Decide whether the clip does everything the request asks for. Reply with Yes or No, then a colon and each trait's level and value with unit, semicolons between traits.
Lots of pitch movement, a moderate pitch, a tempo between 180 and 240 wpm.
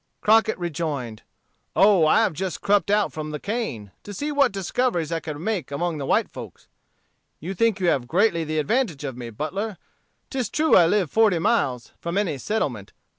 Yes: wide, 5.8 semitones; medium, 175 Hz; average, 185 wpm